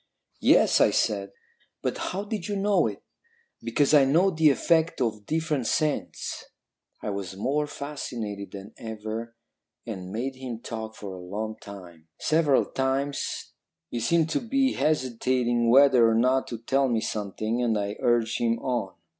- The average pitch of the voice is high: No, low, 120 Hz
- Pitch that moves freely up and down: No, average, 4.9 semitones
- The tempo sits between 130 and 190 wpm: Yes, average, 155 wpm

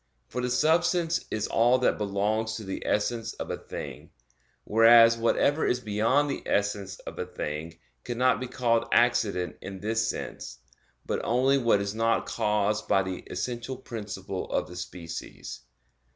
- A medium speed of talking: Yes, average, 155 wpm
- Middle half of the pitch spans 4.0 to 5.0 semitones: No, average, 3.6 semitones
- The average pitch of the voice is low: Yes, low, 115 Hz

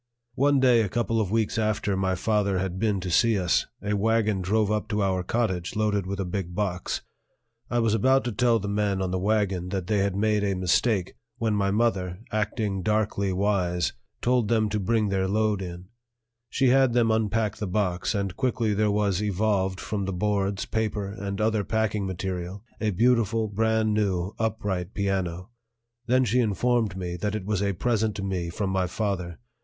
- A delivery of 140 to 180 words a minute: No, average, 190 wpm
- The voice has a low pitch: Yes, low, 105 Hz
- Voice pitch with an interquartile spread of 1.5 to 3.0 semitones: Yes, average, 2.7 semitones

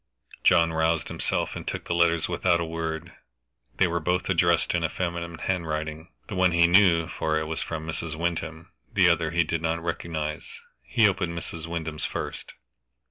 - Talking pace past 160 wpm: Yes, average, 175 wpm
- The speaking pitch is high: No, very low, 85 Hz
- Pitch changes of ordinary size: No, narrow, 1.3 semitones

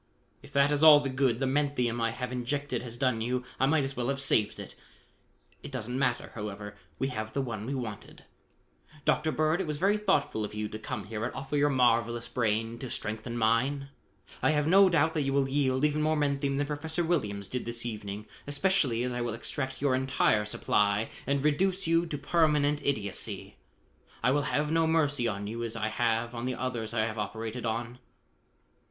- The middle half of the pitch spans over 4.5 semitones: No, average, 4.1 semitones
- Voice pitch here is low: Yes, low, 130 Hz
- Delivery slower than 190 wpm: No, fast, 205 wpm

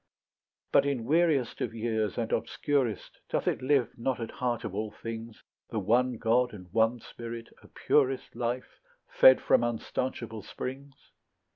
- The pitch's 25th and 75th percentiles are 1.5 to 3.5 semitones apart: Yes, narrow, 2.6 semitones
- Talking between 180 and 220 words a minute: No, average, 150 wpm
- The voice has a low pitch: Yes, low, 120 Hz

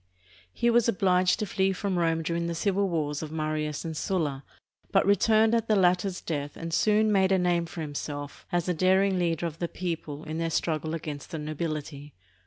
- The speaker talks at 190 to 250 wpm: Yes, average, 195 wpm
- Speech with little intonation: No, average, 3.6 semitones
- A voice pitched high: No, medium, 170 Hz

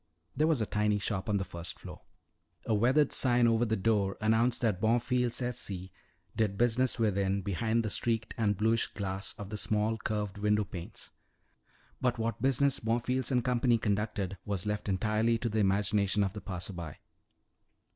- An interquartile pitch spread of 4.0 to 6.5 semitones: No, average, 2.7 semitones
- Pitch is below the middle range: Yes, low, 110 Hz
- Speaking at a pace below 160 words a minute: No, average, 175 wpm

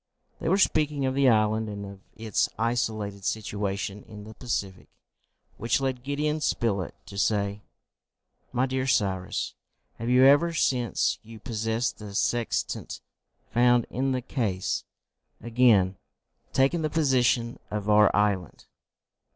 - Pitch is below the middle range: Yes, low, 115 Hz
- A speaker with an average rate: No, slow, 130 wpm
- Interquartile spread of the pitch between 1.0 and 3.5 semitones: No, average, 4.1 semitones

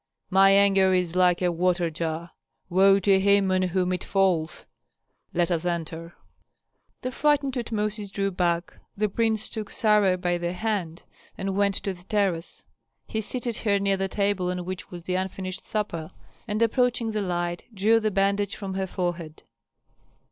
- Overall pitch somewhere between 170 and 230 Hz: Yes, high, 190 Hz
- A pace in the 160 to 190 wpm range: Yes, average, 165 wpm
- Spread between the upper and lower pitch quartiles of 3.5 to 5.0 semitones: No, average, 2.7 semitones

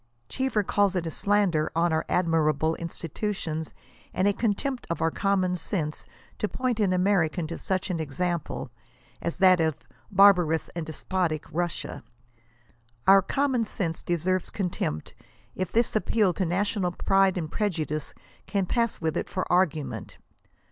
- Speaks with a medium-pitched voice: Yes, medium, 180 Hz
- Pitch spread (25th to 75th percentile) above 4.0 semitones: No, average, 3.6 semitones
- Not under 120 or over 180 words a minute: Yes, average, 155 wpm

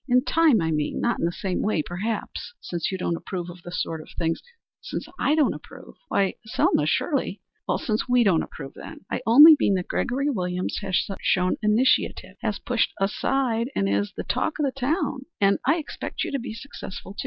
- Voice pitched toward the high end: Yes, high, 210 Hz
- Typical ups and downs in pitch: No, wide, 6.2 semitones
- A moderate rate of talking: No, fast, 210 wpm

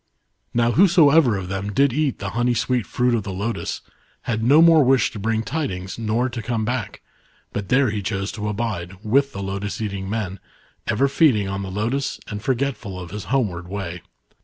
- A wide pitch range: No, average, 4.6 semitones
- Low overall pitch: Yes, low, 110 Hz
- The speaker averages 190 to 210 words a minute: Yes, average, 195 wpm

